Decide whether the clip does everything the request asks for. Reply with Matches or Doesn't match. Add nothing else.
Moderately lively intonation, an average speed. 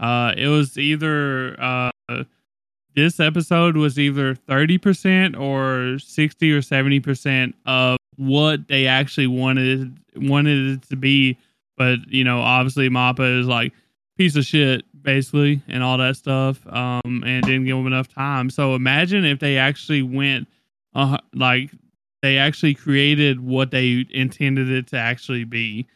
Doesn't match